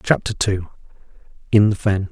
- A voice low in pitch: Yes, low, 100 Hz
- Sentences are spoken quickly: No, slow, 115 wpm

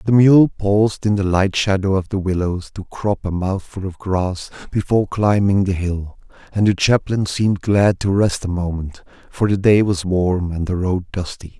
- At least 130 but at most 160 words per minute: No, average, 195 wpm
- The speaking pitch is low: Yes, very low, 95 Hz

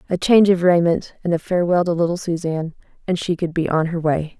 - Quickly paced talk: Yes, fast, 230 wpm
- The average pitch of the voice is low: No, medium, 170 Hz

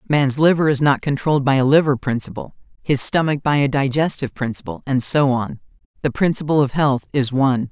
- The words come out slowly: No, average, 185 wpm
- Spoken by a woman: Yes, female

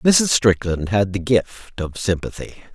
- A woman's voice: No, male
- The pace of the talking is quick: No, average, 155 wpm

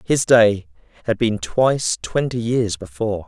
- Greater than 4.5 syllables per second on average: No, 4.4 syllables/s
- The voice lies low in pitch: Yes, low, 110 Hz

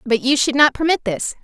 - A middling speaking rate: No, fast, 250 wpm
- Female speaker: Yes, female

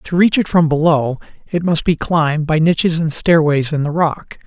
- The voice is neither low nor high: Yes, medium, 160 Hz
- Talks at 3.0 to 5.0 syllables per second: Yes, 4.9 syllables/s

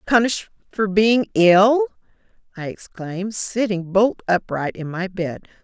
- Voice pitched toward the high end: Yes, high, 200 Hz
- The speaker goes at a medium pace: No, slow, 130 wpm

